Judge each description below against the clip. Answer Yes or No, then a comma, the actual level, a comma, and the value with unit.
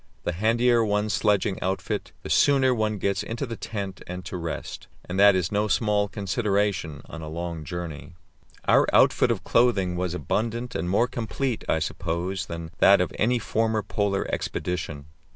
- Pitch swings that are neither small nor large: Yes, average, 4.0 semitones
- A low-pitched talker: Yes, low, 100 Hz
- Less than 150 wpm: No, average, 170 wpm